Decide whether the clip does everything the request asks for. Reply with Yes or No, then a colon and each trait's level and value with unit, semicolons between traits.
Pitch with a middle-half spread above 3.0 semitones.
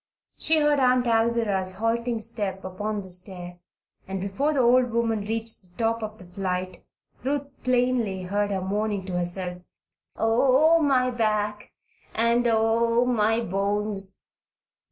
Yes: average, 3.8 semitones